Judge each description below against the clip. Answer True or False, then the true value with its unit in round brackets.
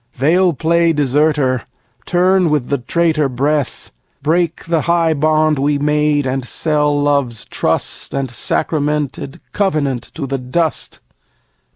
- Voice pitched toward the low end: False (150 Hz)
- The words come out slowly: True (120 wpm)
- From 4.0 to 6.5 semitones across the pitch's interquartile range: False (2.9 semitones)